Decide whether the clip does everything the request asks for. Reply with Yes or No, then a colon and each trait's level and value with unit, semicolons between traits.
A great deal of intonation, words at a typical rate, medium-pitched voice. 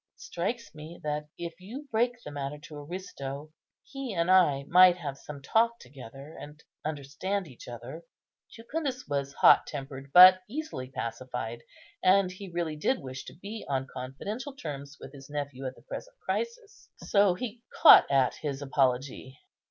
Yes: wide, 6.5 semitones; average, 160 wpm; medium, 150 Hz